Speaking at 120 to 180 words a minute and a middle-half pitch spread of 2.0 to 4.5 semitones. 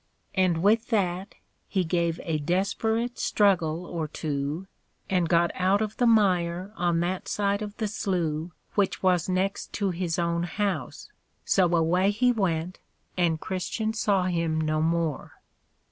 Yes: average, 145 wpm; average, 3.1 semitones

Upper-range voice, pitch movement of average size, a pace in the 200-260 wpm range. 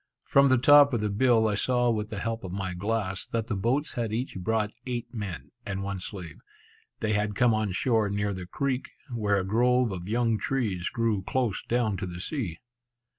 No: low, 110 Hz; average, 3.6 semitones; fast, 205 wpm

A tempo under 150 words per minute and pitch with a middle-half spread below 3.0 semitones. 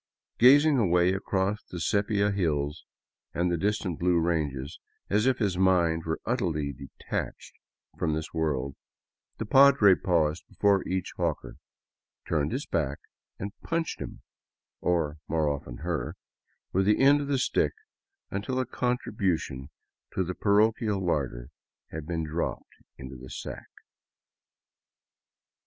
No: slow, 135 wpm; average, 5.2 semitones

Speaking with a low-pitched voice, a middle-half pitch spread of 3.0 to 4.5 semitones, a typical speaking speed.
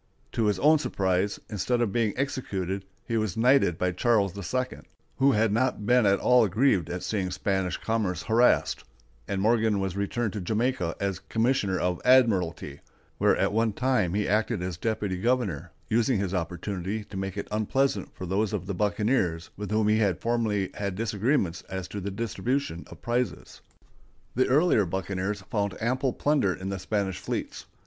Yes: low, 105 Hz; average, 3.7 semitones; average, 170 wpm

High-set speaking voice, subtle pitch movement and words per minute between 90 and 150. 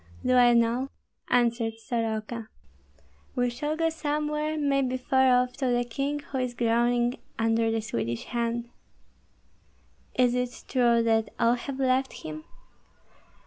Yes: high, 245 Hz; narrow, 2.3 semitones; slow, 135 wpm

